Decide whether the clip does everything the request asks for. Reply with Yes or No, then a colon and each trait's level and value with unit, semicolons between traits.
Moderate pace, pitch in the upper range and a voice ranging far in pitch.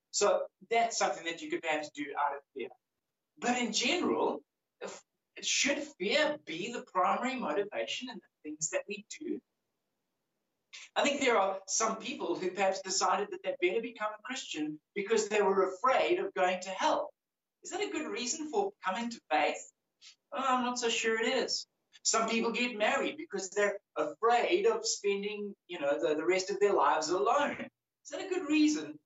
Yes: average, 185 wpm; high, 225 Hz; wide, 7.0 semitones